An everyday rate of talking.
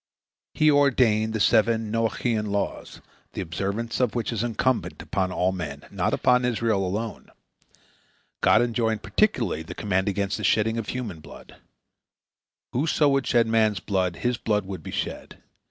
Yes: average, 155 wpm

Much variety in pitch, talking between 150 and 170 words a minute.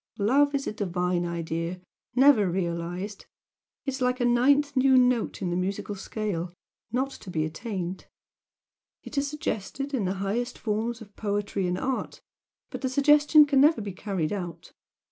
Yes: wide, 6.5 semitones; average, 165 wpm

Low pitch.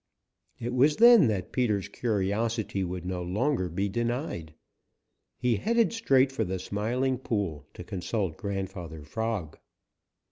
Yes: low, 105 Hz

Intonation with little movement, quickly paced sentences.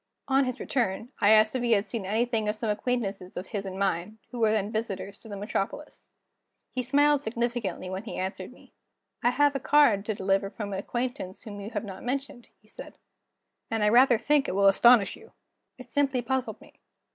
No: average, 3.9 semitones; fast, 210 wpm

